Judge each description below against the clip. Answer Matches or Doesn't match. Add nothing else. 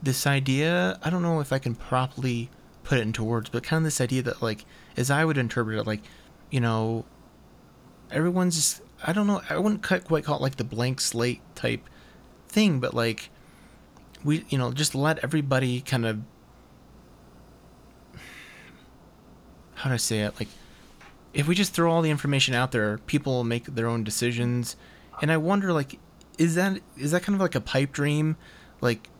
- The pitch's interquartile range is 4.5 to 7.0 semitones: Matches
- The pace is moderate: Matches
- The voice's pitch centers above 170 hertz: Doesn't match